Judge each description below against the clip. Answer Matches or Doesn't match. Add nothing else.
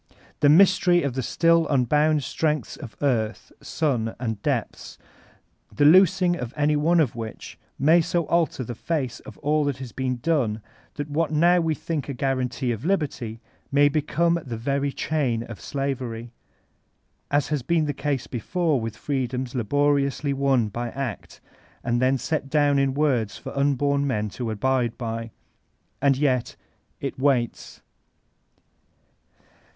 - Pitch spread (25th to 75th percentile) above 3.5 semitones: Matches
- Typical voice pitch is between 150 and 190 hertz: Doesn't match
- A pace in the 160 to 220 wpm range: Doesn't match